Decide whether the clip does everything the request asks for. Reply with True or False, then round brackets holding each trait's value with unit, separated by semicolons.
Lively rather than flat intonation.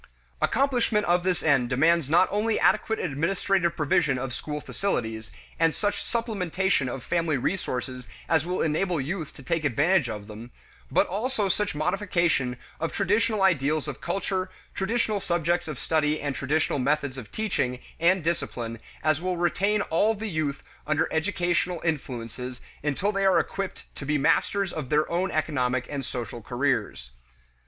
True (5.8 semitones)